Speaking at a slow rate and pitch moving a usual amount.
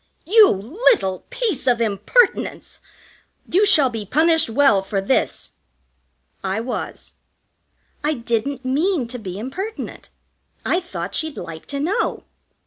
No: slow, 125 wpm; wide, 7.7 semitones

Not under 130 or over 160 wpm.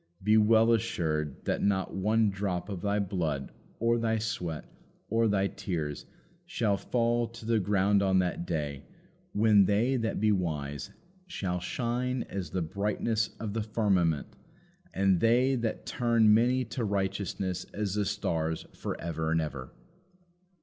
Yes: average, 150 wpm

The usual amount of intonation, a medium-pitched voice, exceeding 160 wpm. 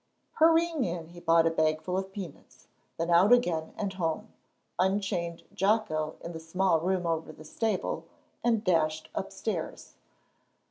No: average, 3.6 semitones; medium, 175 Hz; average, 140 wpm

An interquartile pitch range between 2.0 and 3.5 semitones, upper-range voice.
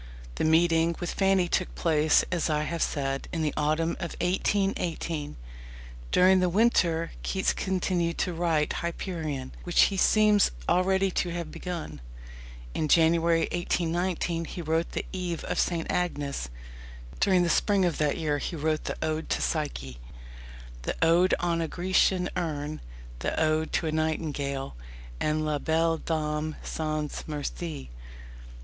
No: narrow, 2.5 semitones; medium, 165 Hz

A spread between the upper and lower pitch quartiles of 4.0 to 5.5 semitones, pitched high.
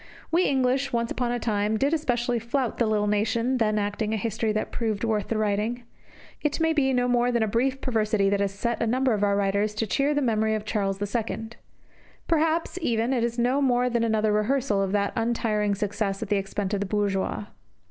No: average, 3.0 semitones; high, 225 Hz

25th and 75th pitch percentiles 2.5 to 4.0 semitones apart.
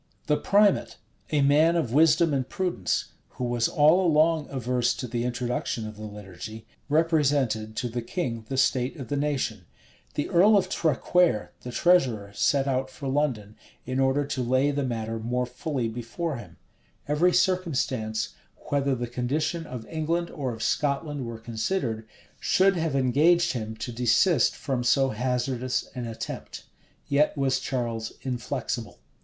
No: average, 4.5 semitones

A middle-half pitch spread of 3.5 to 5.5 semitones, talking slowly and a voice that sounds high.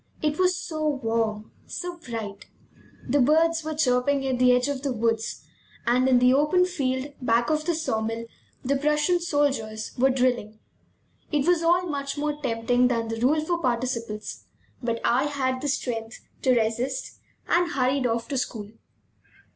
No: average, 4.4 semitones; average, 165 wpm; very high, 260 Hz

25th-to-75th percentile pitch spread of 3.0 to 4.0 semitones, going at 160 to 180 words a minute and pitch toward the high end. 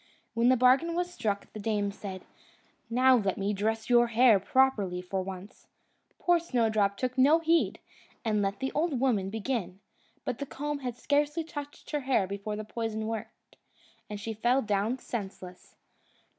No: average, 4.7 semitones; average, 165 wpm; high, 225 Hz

